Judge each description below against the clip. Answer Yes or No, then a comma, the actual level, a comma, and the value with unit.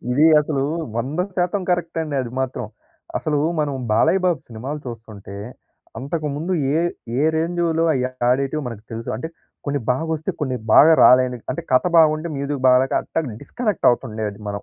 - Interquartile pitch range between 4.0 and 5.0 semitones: Yes, average, 4.5 semitones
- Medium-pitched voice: Yes, medium, 145 Hz